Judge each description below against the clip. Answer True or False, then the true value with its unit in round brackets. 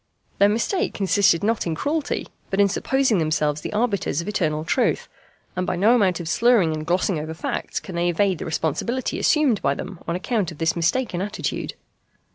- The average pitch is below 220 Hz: True (185 Hz)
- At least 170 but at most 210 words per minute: True (190 wpm)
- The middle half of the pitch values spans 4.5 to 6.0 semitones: True (5.2 semitones)